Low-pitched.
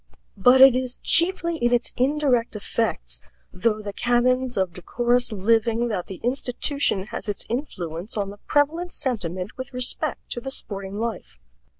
No: high, 240 Hz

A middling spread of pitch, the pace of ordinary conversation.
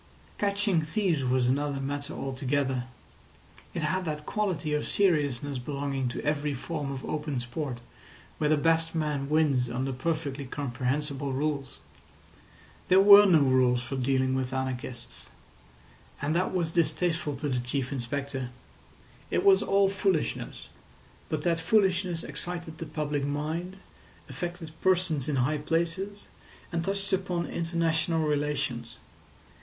No: average, 3.9 semitones; slow, 130 wpm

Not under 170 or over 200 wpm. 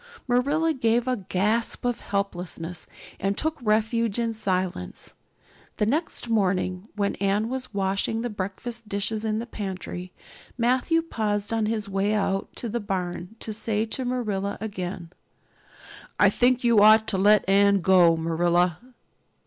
No: average, 145 wpm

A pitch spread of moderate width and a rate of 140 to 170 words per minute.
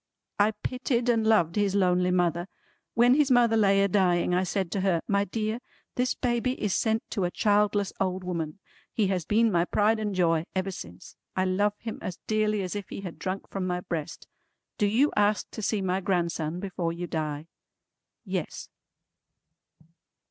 No: average, 3.3 semitones; average, 180 wpm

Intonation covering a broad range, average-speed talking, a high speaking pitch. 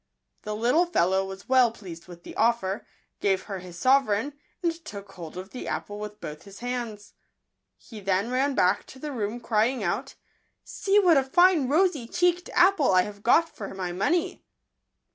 Yes: wide, 6.2 semitones; average, 180 wpm; high, 225 Hz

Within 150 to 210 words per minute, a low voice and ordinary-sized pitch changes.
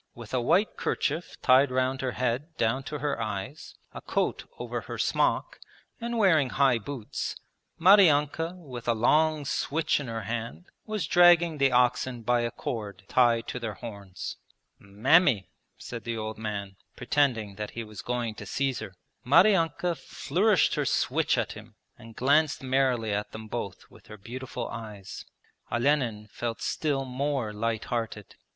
Yes: average, 160 wpm; low, 125 Hz; average, 4.7 semitones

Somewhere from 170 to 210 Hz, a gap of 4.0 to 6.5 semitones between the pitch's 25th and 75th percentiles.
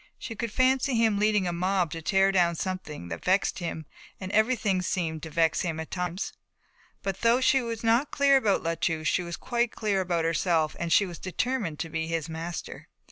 Yes: medium, 185 Hz; average, 4.9 semitones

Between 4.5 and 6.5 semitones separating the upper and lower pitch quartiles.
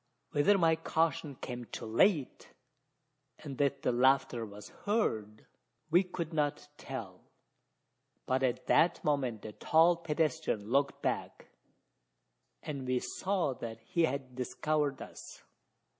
Yes: average, 4.8 semitones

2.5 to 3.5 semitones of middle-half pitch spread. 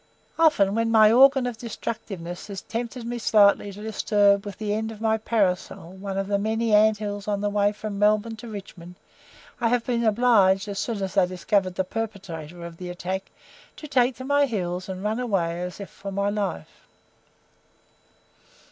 Yes: average, 2.8 semitones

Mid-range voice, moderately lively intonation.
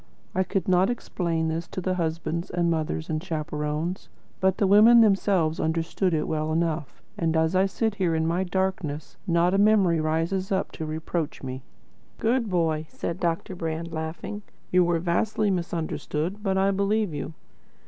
Yes: medium, 170 Hz; average, 3.0 semitones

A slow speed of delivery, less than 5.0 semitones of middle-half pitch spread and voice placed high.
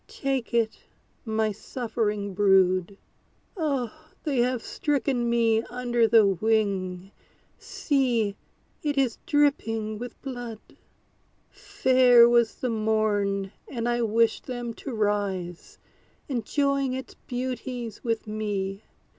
Yes: slow, 105 wpm; average, 3.2 semitones; high, 230 Hz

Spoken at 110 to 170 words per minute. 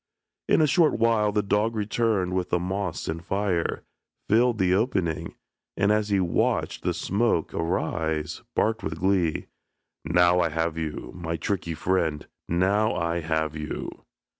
Yes: average, 150 wpm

